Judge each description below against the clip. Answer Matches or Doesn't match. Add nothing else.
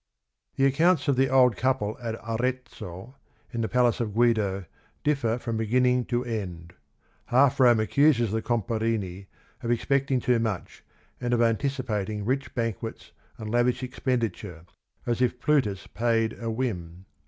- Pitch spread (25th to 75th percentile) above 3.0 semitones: Doesn't match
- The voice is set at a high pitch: Doesn't match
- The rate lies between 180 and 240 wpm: Doesn't match